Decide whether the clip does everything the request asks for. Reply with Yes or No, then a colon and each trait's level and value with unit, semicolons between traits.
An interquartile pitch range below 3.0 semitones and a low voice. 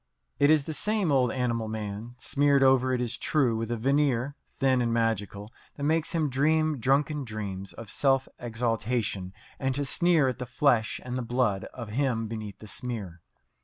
No: average, 3.8 semitones; low, 125 Hz